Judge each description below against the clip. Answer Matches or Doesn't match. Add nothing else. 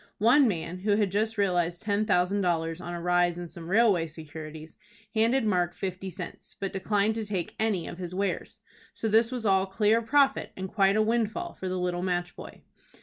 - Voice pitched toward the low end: Doesn't match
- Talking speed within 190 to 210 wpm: Matches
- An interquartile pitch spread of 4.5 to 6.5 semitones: Doesn't match